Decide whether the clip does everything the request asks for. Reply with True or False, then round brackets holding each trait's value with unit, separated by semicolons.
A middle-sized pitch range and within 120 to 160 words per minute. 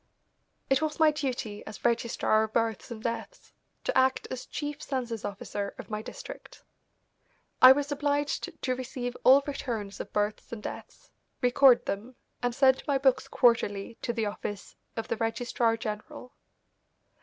True (3.5 semitones; 155 wpm)